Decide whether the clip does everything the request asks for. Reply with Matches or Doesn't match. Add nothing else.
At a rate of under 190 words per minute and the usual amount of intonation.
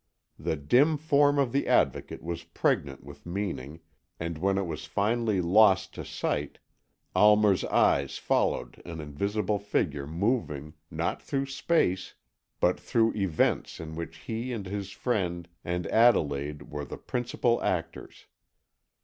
Doesn't match